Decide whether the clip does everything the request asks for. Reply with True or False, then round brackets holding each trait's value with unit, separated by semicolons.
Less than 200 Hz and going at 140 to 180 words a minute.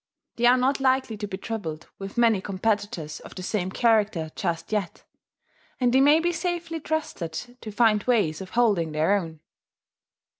False (215 Hz; 165 wpm)